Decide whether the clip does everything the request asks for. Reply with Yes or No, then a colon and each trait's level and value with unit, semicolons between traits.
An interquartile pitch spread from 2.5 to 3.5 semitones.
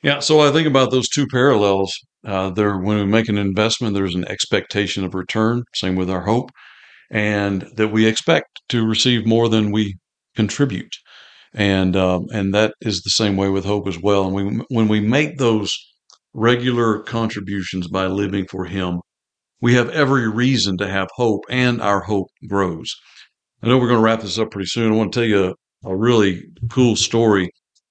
Yes: average, 3.2 semitones